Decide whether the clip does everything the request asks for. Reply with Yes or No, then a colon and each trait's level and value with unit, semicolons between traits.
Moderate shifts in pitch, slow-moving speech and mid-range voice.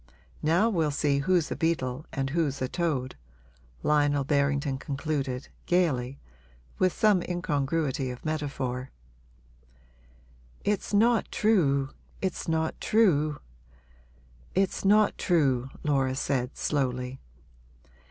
Yes: average, 4.3 semitones; slow, 105 wpm; medium, 145 Hz